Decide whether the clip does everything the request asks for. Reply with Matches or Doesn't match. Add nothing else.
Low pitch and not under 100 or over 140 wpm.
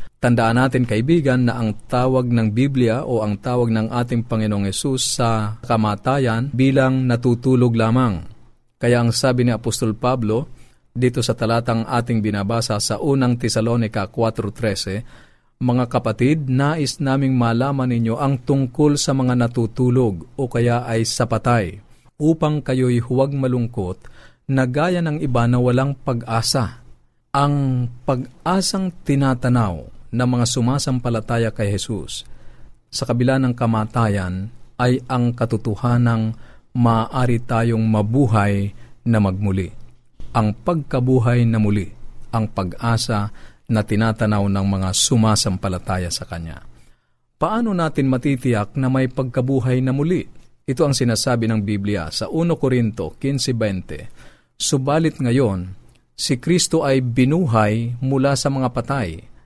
Matches